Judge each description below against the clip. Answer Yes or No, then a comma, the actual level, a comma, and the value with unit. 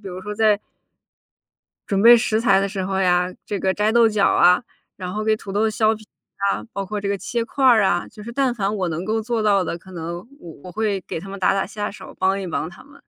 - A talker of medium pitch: No, high, 200 Hz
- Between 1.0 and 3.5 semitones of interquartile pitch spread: Yes, average, 2.7 semitones